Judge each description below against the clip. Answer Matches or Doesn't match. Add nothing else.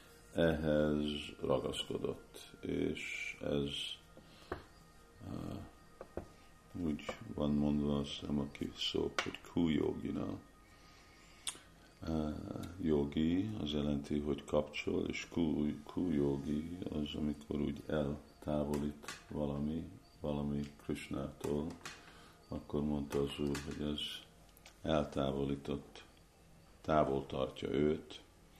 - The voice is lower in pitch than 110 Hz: Matches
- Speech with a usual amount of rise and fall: Doesn't match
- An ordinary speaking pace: Doesn't match